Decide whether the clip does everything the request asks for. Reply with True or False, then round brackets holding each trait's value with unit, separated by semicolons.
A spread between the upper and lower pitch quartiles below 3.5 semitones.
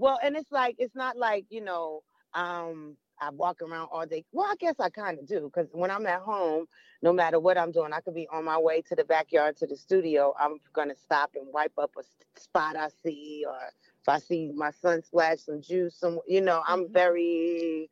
True (2.8 semitones)